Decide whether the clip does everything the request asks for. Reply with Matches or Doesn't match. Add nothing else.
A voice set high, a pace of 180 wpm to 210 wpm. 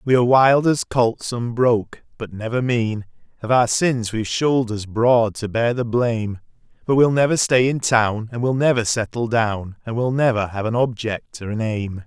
Doesn't match